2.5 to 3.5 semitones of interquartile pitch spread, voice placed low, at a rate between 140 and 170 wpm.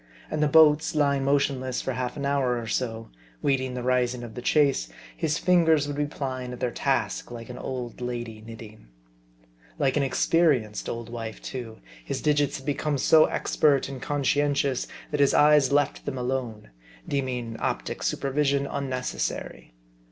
Yes: average, 2.9 semitones; low, 130 Hz; average, 160 wpm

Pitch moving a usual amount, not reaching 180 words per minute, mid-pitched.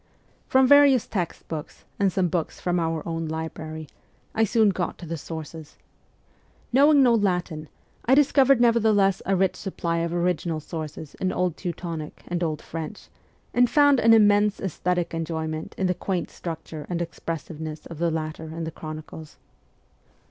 Yes: average, 4.2 semitones; average, 155 wpm; medium, 175 Hz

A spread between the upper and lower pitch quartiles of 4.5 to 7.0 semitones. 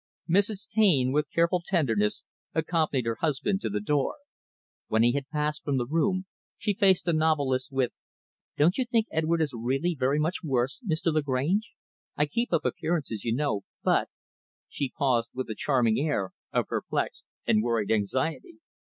Yes: average, 4.9 semitones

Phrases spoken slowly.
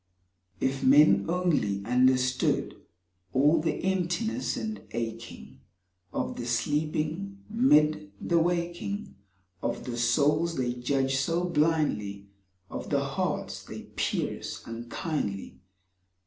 Yes: slow, 105 wpm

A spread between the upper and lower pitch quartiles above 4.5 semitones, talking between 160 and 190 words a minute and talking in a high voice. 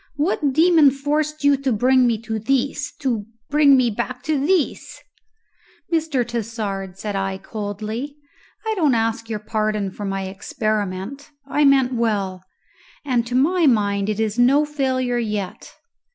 No: average, 5.0 semitones; average, 150 wpm; high, 240 Hz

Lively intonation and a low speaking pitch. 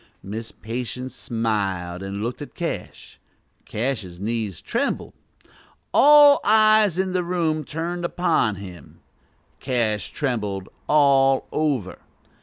Yes: wide, 8.0 semitones; low, 125 Hz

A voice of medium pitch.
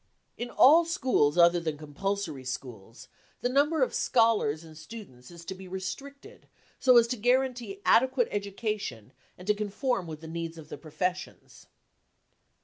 No: high, 195 Hz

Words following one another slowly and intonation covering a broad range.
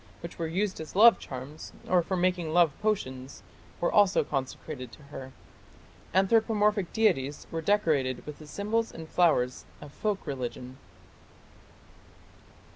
Yes: slow, 130 wpm; wide, 6.4 semitones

